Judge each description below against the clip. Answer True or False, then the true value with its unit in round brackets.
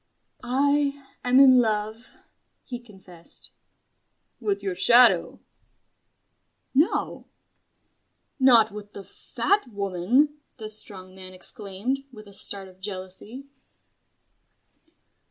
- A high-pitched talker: True (215 Hz)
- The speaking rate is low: True (95 wpm)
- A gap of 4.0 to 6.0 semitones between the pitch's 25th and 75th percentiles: True (4.7 semitones)